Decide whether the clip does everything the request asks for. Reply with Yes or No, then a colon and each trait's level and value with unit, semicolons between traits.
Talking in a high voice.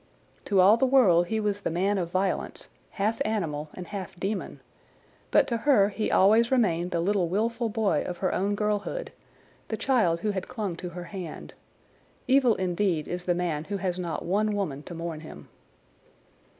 Yes: high, 195 Hz